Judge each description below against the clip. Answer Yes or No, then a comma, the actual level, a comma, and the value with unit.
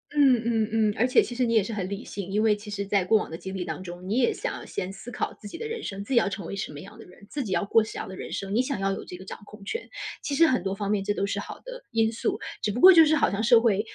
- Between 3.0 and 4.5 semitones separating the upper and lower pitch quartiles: Yes, average, 3.6 semitones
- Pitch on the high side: Yes, high, 210 Hz